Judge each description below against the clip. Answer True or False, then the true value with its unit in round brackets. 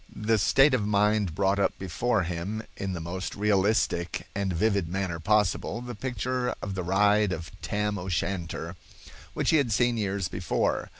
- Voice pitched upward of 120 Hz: False (100 Hz)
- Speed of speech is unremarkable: True (165 wpm)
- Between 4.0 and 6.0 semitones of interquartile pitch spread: False (2.9 semitones)